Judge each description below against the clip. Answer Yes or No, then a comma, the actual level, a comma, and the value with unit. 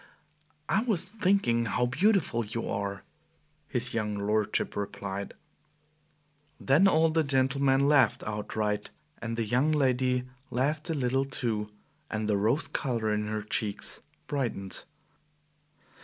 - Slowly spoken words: Yes, slow, 125 wpm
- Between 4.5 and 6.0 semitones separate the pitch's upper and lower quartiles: Yes, average, 4.9 semitones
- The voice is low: Yes, low, 125 Hz